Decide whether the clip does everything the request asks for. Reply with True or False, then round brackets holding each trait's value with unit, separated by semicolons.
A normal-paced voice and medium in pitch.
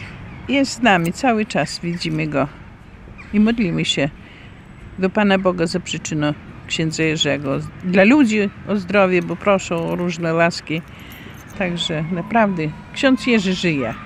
True (130 wpm; 175 Hz)